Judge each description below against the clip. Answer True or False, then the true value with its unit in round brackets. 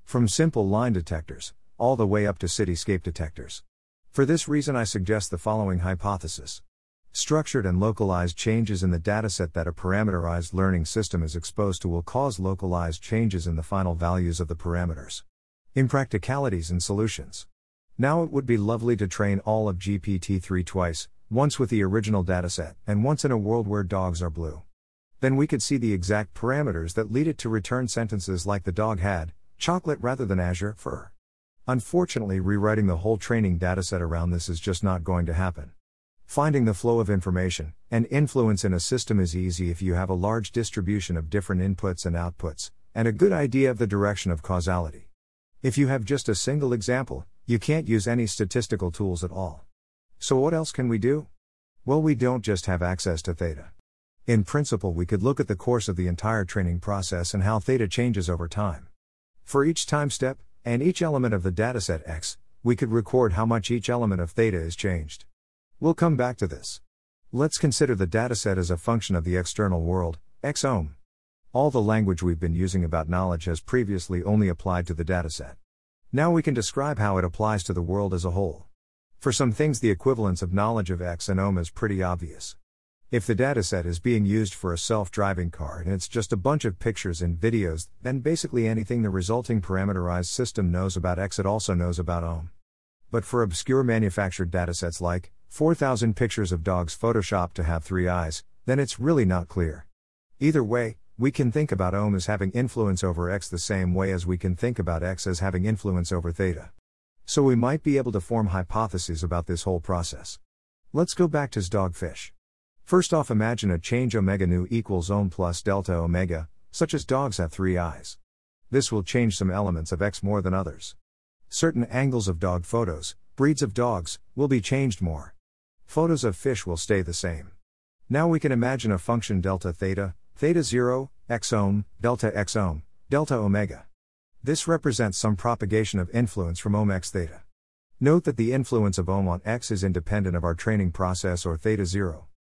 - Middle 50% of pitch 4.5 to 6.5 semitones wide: True (4.9 semitones)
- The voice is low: True (100 Hz)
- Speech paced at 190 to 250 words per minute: True (195 wpm)